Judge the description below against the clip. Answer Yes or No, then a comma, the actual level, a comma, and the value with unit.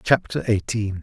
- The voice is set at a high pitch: No, low, 110 Hz